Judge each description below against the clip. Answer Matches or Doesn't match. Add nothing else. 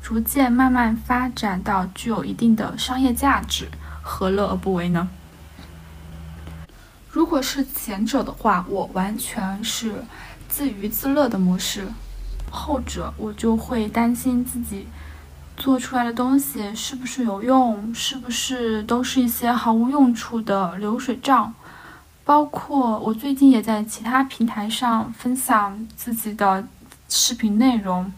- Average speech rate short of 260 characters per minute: Matches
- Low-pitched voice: Doesn't match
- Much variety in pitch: Doesn't match